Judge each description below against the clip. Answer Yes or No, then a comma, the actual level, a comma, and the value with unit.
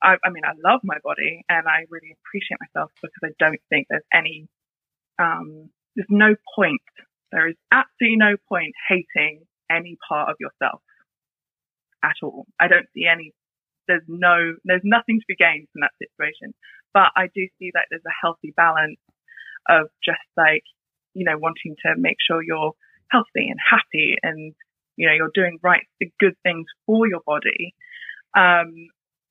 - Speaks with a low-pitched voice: No, medium, 170 Hz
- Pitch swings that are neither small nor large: Yes, average, 3.4 semitones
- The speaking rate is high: No, average, 170 wpm